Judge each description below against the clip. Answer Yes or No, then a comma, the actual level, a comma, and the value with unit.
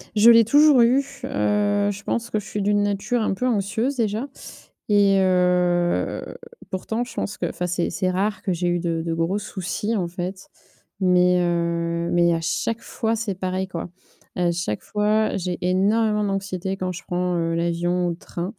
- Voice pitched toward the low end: No, high, 190 Hz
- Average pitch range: Yes, average, 3.1 semitones